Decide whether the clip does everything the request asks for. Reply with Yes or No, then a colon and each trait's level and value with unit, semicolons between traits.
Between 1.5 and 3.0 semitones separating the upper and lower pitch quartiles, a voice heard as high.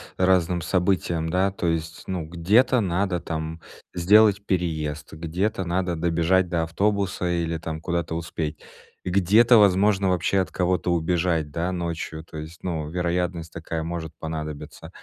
No: narrow, 2.4 semitones; very low, 85 Hz